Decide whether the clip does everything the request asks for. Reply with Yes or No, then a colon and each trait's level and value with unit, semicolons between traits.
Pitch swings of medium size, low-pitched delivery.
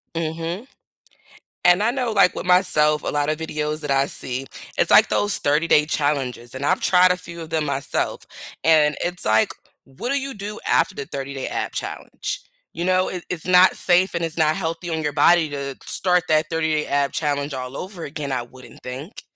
No: average, 4.0 semitones; medium, 155 Hz